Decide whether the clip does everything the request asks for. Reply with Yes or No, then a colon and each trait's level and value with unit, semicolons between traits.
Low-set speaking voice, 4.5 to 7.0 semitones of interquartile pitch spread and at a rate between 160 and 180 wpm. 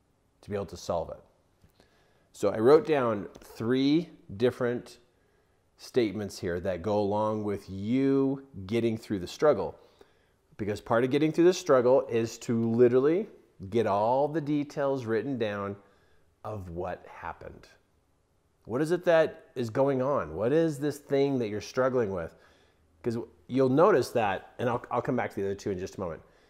Yes: low, 120 Hz; average, 5.1 semitones; average, 170 wpm